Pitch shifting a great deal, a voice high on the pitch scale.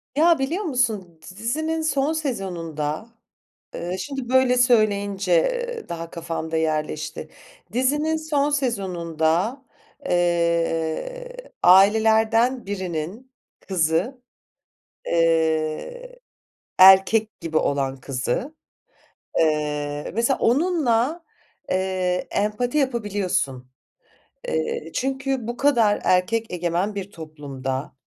Yes: wide, 7.9 semitones; high, 200 Hz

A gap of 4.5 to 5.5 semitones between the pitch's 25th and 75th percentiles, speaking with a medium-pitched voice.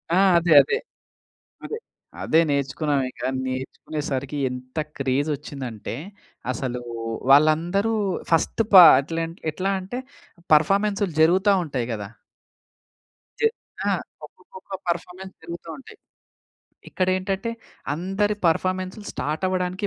Yes: average, 5.1 semitones; medium, 165 Hz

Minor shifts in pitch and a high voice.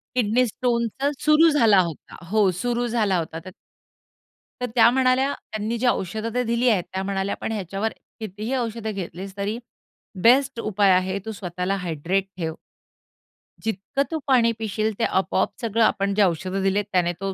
No: average, 3.7 semitones; high, 215 Hz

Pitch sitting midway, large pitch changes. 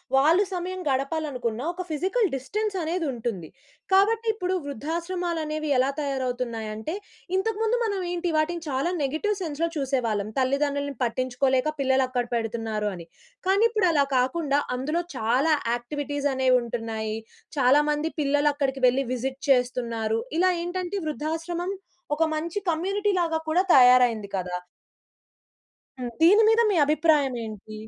No: very high, 285 Hz; wide, 5.7 semitones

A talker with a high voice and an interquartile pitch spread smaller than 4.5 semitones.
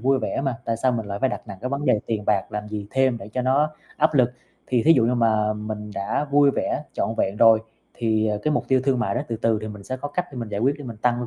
No: low, 115 Hz; average, 3.7 semitones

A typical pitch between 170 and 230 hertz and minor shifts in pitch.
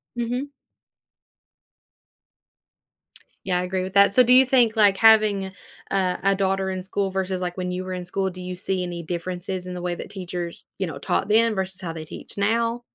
Yes: high, 190 Hz; narrow, 2.1 semitones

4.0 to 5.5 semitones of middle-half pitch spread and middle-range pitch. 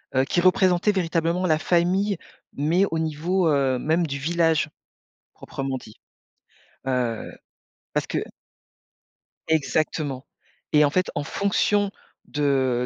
Yes: average, 4.3 semitones; medium, 160 Hz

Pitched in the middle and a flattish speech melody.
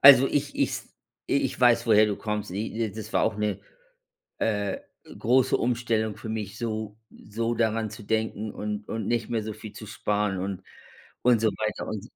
No: low, 110 Hz; narrow, 1.6 semitones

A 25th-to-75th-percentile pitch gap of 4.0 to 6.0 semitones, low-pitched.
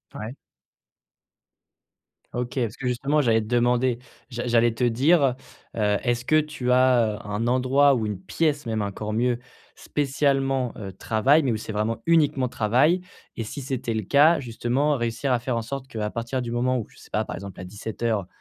No: average, 3.3 semitones; low, 120 Hz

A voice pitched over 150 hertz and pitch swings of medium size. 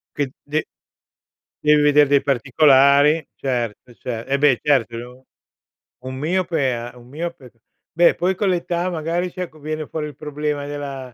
No: medium, 145 Hz; average, 3.3 semitones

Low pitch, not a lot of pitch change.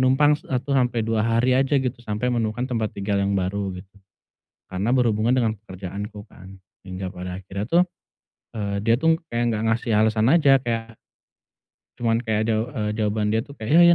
No: low, 115 Hz; average, 3.3 semitones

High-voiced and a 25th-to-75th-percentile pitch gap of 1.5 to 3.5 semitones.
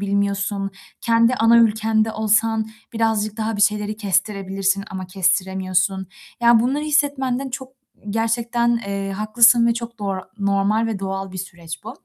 Yes: high, 215 Hz; average, 2.8 semitones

